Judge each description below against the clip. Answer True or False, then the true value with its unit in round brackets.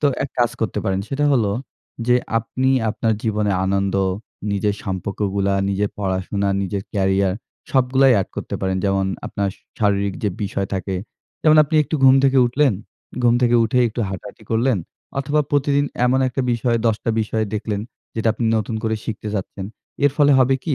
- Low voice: True (110 Hz)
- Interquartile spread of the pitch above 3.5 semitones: True (4.7 semitones)